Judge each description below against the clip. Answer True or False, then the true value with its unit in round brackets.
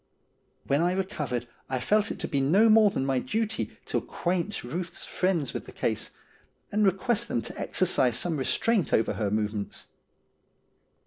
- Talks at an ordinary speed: True (165 wpm)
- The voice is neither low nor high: True (170 Hz)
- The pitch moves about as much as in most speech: False (8.5 semitones)